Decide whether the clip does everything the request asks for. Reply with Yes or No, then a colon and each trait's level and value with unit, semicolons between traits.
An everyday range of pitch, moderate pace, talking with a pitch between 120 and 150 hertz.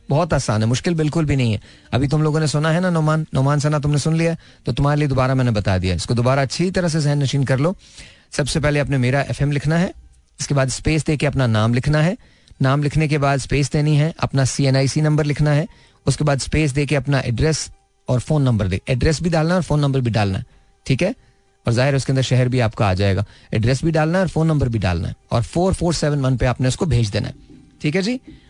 Yes: average, 3.6 semitones; average, 145 wpm; medium, 140 Hz